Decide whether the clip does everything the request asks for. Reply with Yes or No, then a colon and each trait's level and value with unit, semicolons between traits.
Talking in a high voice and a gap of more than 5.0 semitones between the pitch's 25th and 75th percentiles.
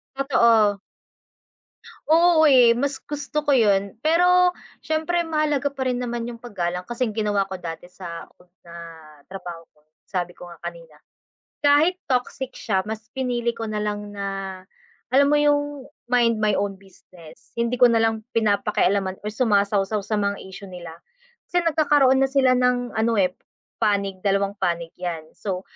Yes: high, 220 Hz; wide, 5.5 semitones